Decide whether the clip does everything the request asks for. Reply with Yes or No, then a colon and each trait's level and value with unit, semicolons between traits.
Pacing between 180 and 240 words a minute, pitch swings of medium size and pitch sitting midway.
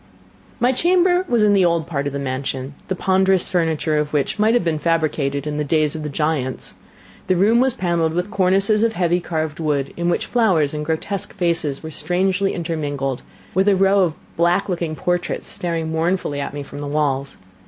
Yes: average, 195 wpm; average, 4.2 semitones; medium, 165 Hz